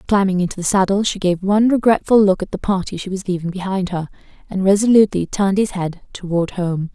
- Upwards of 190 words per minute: Yes, fast, 205 wpm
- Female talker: Yes, female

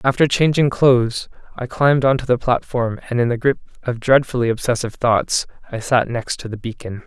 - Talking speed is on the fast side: No, average, 185 wpm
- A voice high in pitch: No, low, 125 Hz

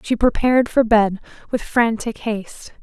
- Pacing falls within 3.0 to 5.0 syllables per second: Yes, 4.7 syllables/s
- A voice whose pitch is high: Yes, high, 225 Hz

